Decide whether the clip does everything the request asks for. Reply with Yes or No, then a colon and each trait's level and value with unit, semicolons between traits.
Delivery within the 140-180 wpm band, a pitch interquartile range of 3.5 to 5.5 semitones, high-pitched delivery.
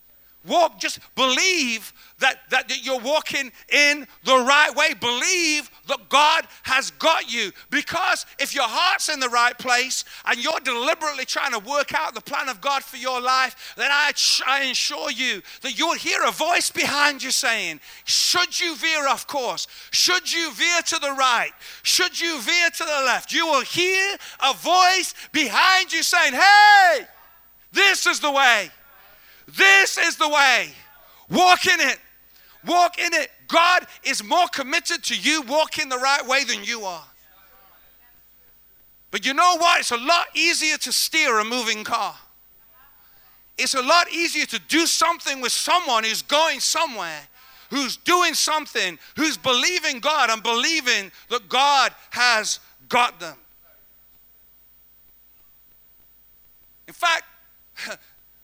Yes: average, 150 wpm; average, 4.5 semitones; very high, 295 Hz